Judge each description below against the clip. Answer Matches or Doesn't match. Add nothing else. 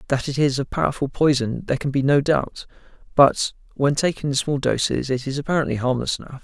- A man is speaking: Matches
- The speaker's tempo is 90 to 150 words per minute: Doesn't match